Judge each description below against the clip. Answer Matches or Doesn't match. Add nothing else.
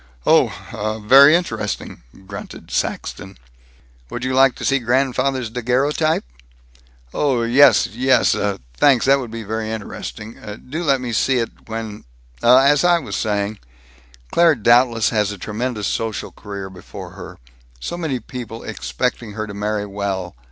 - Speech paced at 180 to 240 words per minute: Doesn't match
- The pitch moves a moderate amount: Matches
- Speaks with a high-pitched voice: Doesn't match